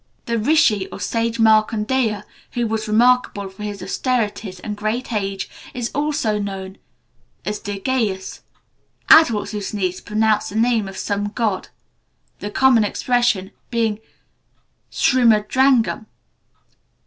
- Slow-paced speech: Yes, slow, 115 wpm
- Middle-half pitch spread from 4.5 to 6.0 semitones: No, average, 2.8 semitones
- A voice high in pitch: Yes, high, 215 Hz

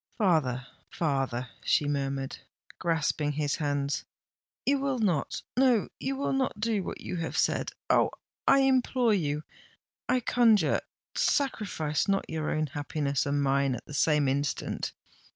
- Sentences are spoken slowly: Yes, slow, 125 wpm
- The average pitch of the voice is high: No, medium, 155 Hz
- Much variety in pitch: Yes, wide, 7.9 semitones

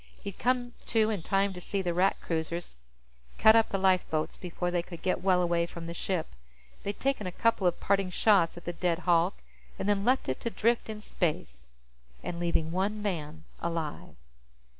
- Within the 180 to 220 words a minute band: Yes, average, 190 wpm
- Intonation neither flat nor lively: Yes, average, 3.2 semitones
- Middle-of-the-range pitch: Yes, medium, 180 Hz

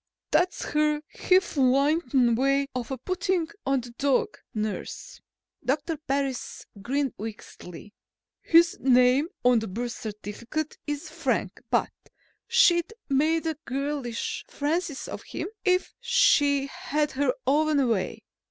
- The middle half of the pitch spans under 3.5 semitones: No, average, 4.2 semitones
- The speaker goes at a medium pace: No, slow, 115 wpm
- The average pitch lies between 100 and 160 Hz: No, very high, 280 Hz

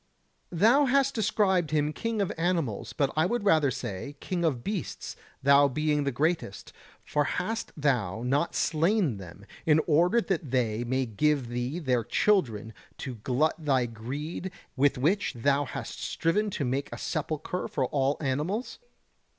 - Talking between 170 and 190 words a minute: No, average, 155 wpm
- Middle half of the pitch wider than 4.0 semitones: Yes, wide, 5.6 semitones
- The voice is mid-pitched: Yes, medium, 150 Hz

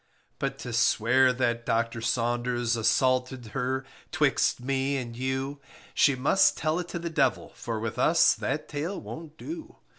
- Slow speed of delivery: No, average, 155 wpm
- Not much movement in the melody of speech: No, average, 3.3 semitones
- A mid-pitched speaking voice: No, low, 130 Hz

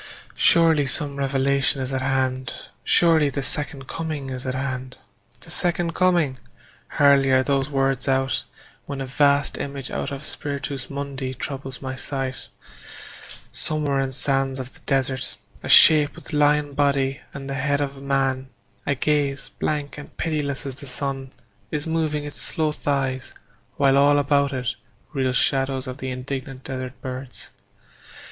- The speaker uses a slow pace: No, average, 155 wpm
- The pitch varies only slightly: Yes, narrow, 1.5 semitones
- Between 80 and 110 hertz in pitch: No, low, 135 Hz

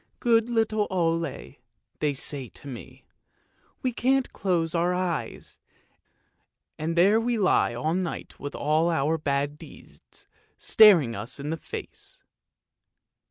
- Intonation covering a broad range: Yes, wide, 6.1 semitones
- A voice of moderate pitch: Yes, medium, 165 Hz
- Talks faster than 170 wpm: No, slow, 135 wpm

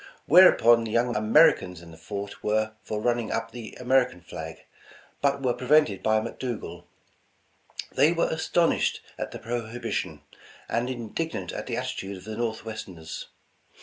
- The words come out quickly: No, average, 155 wpm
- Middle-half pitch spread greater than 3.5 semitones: No, average, 3.2 semitones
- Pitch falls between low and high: No, low, 115 Hz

